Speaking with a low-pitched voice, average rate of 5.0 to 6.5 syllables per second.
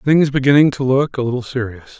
Yes: low, 130 Hz; 5.6 syllables/s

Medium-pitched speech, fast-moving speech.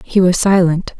No: medium, 180 Hz; average, 180 wpm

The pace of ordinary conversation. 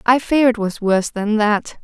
No: fast, 230 wpm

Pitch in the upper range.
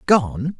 No: medium, 145 Hz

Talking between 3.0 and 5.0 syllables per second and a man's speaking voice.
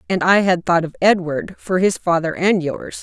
No: 4.7 syllables/s; female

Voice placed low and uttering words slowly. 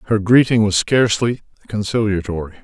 Yes: low, 105 Hz; slow, 115 wpm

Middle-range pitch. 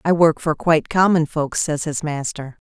Yes: medium, 155 Hz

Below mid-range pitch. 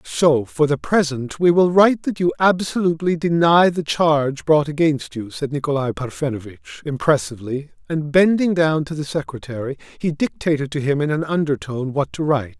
No: medium, 150 Hz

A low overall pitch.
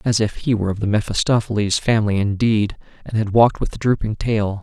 Yes: low, 105 Hz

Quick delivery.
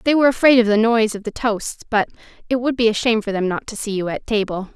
Yes: fast, 290 wpm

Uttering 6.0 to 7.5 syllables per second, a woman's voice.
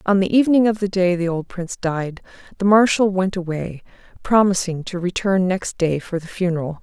No: 5.4 syllables/s; female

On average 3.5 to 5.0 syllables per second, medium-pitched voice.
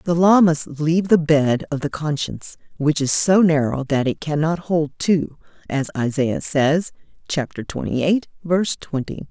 Yes: 4.5 syllables/s; medium, 155 Hz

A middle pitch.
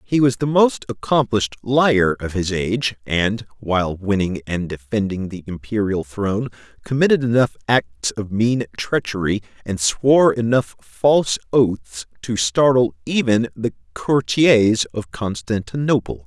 No: low, 110 Hz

